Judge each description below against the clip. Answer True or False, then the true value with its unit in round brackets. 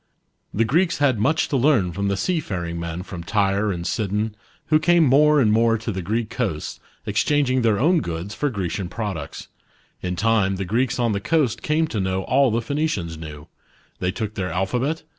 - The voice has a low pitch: True (110 Hz)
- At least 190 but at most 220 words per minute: True (200 wpm)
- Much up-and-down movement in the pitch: True (6.2 semitones)